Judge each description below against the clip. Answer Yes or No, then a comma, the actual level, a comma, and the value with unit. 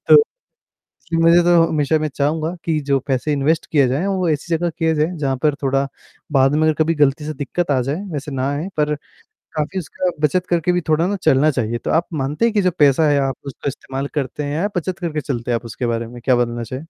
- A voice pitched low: No, medium, 150 Hz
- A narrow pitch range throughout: No, average, 3.4 semitones